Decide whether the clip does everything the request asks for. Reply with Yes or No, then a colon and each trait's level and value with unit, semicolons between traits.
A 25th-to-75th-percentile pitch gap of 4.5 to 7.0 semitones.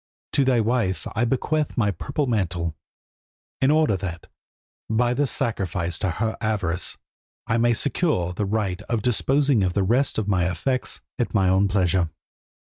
Yes: average, 5.0 semitones